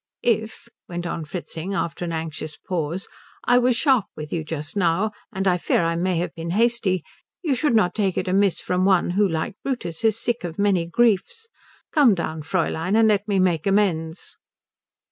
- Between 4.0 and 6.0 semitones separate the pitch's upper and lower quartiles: Yes, average, 4.5 semitones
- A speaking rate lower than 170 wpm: No, average, 185 wpm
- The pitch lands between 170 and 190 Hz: Yes, medium, 185 Hz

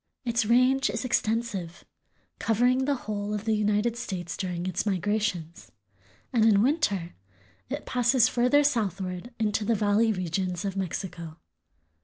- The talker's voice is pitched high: Yes, high, 210 Hz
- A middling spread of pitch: Yes, average, 4.1 semitones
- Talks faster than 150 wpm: No, slow, 135 wpm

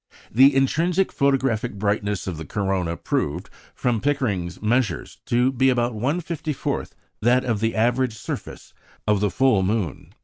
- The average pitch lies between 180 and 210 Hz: No, low, 115 Hz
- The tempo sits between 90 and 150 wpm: Yes, average, 140 wpm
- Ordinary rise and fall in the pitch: Yes, average, 4.7 semitones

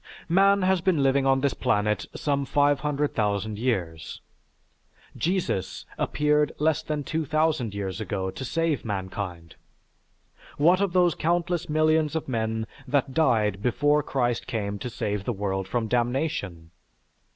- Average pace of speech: No, slow, 130 wpm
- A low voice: Yes, low, 130 Hz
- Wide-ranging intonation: Yes, wide, 6.8 semitones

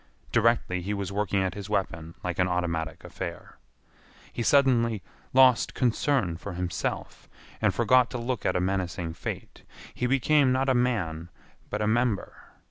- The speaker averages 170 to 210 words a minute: No, average, 155 wpm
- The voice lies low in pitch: Yes, low, 105 Hz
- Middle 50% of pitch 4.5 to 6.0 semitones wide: Yes, wide, 5.6 semitones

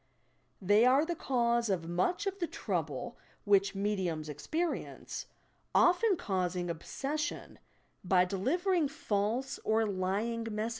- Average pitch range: No, wide, 7.2 semitones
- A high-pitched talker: Yes, high, 215 Hz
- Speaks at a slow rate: Yes, slow, 120 wpm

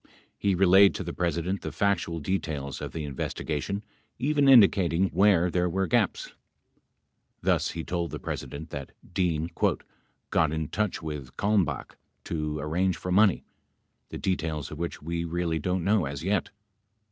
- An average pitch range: Yes, average, 3.4 semitones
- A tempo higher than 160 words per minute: No, average, 150 wpm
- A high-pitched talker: No, very low, 85 Hz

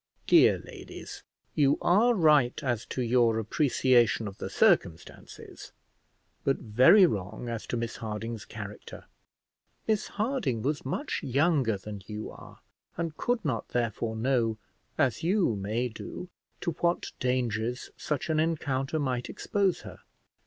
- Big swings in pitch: Yes, wide, 5.8 semitones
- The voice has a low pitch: Yes, low, 125 Hz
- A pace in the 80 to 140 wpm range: Yes, slow, 135 wpm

